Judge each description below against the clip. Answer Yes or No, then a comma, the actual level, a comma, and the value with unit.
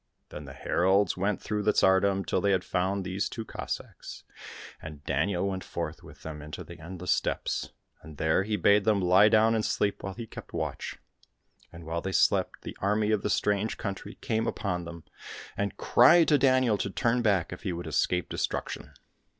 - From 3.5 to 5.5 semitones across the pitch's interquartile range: No, average, 3.1 semitones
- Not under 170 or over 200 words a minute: Yes, average, 190 wpm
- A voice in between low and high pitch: No, low, 100 Hz